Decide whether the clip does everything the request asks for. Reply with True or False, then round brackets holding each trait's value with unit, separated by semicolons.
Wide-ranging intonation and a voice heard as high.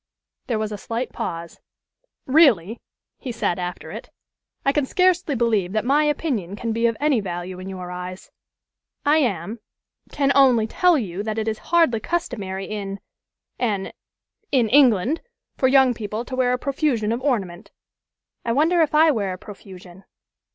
True (6.0 semitones; 230 Hz)